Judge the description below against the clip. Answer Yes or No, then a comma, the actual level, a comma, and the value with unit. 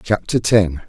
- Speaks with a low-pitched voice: Yes, low, 100 Hz